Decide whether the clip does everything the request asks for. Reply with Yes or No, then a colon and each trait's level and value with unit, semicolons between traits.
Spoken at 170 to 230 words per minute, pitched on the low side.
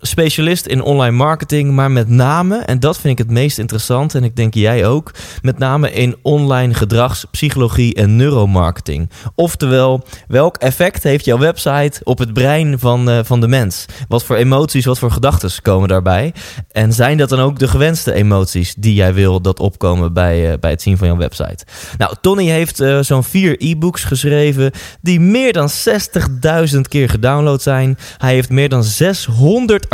Yes: average, 180 wpm; low, 130 Hz